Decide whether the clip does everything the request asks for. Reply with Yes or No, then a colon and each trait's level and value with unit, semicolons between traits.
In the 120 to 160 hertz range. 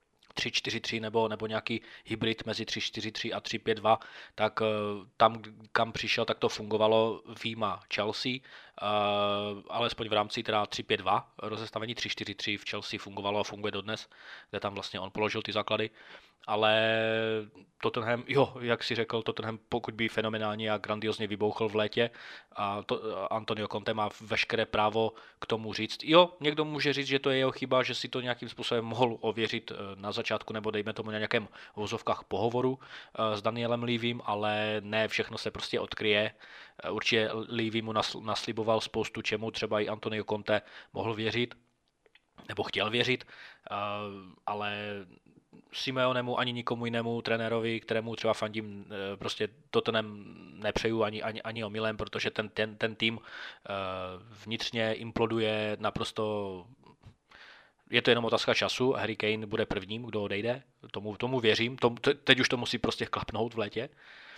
No: low, 110 Hz